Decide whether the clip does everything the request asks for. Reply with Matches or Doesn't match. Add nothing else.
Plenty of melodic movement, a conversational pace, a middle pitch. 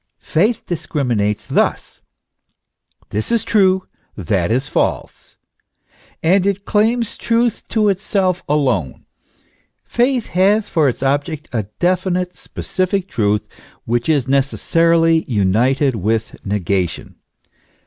Doesn't match